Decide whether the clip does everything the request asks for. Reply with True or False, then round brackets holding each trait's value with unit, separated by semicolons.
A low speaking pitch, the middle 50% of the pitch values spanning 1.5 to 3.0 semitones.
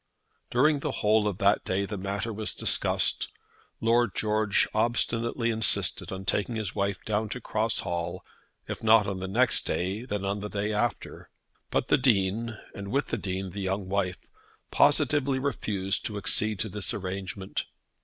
True (105 Hz; 2.7 semitones)